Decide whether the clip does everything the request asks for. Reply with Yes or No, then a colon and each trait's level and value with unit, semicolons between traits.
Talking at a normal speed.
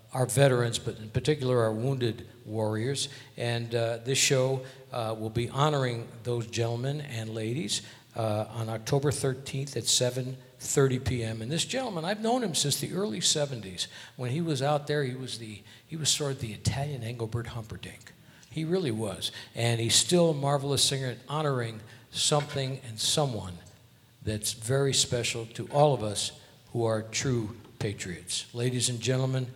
Yes: average, 165 wpm